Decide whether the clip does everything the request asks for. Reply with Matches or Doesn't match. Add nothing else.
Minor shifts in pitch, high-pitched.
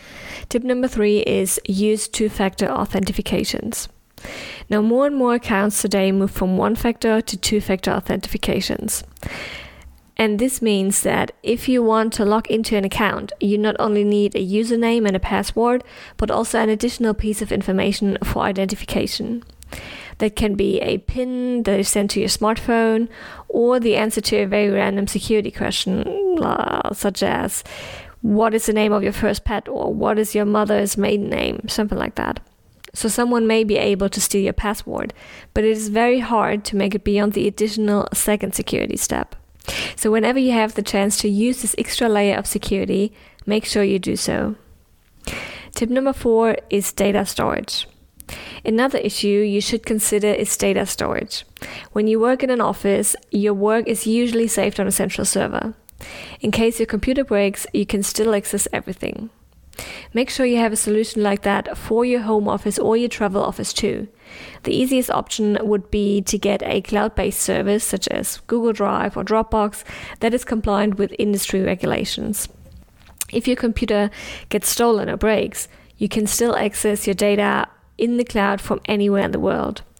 Matches